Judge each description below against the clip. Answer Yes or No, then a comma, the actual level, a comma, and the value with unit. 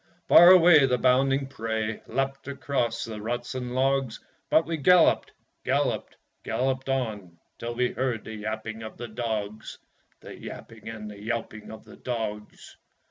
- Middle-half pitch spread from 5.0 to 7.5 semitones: No, average, 3.4 semitones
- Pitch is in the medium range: No, low, 120 Hz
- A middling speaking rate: Yes, average, 150 wpm